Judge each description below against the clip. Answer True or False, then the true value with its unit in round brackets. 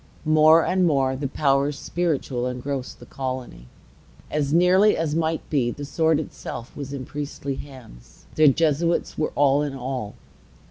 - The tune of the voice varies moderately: True (3.0 semitones)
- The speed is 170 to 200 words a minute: False (150 wpm)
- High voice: False (140 Hz)